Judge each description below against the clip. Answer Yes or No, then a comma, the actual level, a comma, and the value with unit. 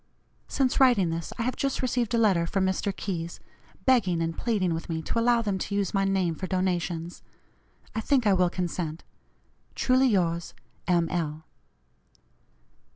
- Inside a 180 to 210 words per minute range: No, average, 160 wpm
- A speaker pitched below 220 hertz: Yes, high, 190 Hz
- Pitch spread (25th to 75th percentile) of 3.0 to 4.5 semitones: No, average, 5.2 semitones